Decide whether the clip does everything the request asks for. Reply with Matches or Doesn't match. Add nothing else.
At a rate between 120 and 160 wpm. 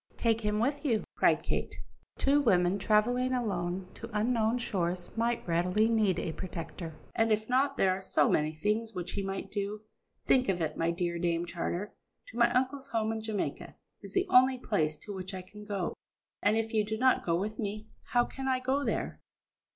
Doesn't match